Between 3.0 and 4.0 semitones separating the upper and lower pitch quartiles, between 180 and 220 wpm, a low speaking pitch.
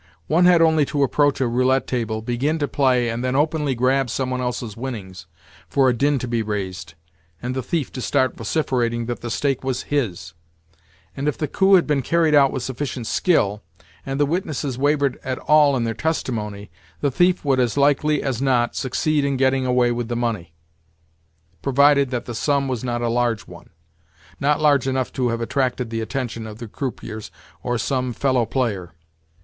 Yes: average, 3.3 semitones; average, 190 wpm; low, 130 Hz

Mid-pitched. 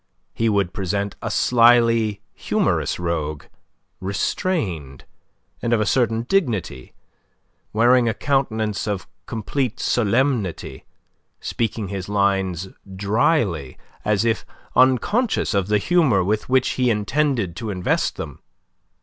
No: low, 110 Hz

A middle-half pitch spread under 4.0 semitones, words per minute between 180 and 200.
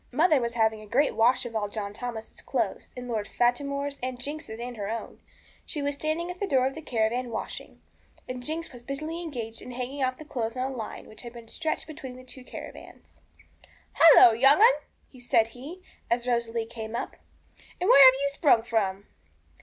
Yes: average, 3.6 semitones; average, 195 wpm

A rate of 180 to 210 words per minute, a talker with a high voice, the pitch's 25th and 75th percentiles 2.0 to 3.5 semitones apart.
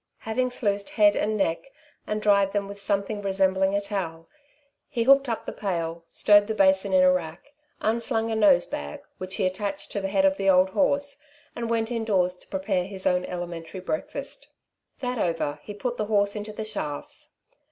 Yes: average, 185 wpm; high, 200 Hz; average, 2.7 semitones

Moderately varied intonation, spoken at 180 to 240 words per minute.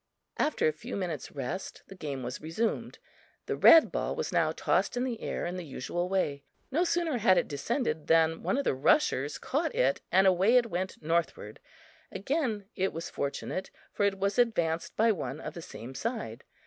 No: wide, 7.0 semitones; average, 190 wpm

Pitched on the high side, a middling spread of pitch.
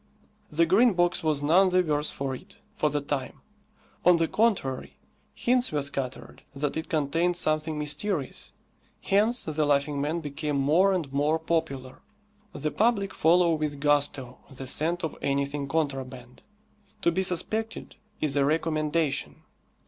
No: medium, 155 Hz; average, 3.7 semitones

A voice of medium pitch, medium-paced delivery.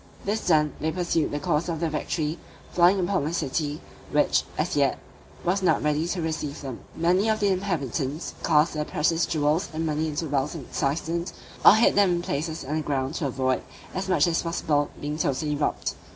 Yes: medium, 160 Hz; average, 190 wpm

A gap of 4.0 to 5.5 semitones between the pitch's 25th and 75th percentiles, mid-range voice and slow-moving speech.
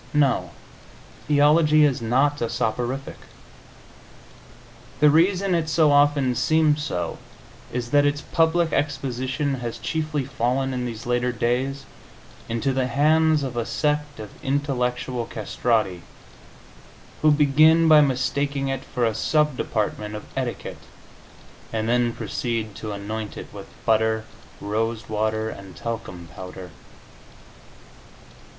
No: average, 4.4 semitones; low, 130 Hz; slow, 120 wpm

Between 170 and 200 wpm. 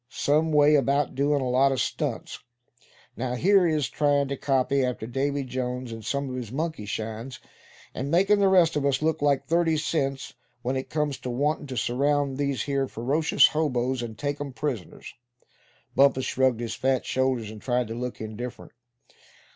Yes: average, 180 wpm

